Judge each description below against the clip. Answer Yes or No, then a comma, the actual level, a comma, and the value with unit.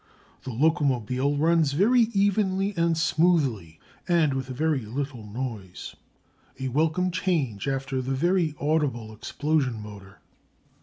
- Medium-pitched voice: Yes, medium, 145 Hz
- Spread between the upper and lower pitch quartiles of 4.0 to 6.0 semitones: Yes, average, 4.9 semitones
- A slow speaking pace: Yes, slow, 115 wpm